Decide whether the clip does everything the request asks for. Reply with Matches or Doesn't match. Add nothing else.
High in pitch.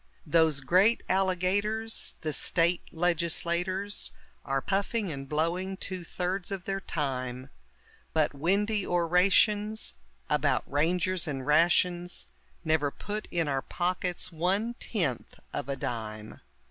Doesn't match